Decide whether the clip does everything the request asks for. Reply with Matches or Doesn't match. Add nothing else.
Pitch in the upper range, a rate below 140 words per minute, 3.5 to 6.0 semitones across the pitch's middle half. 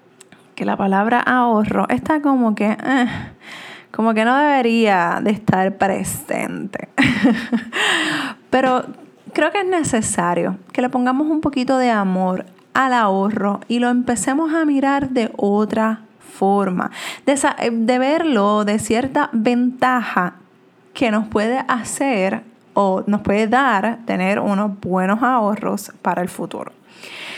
Matches